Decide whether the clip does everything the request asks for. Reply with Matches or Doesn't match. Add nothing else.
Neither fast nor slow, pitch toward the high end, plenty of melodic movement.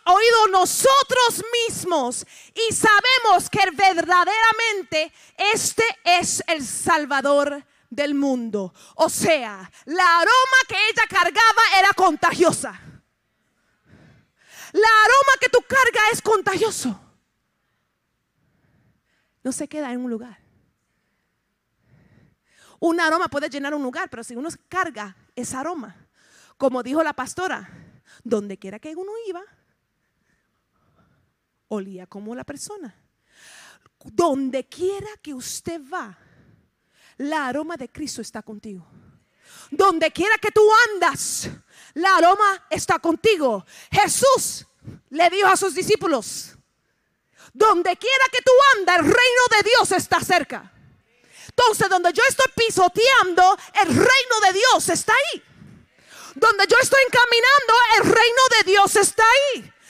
Doesn't match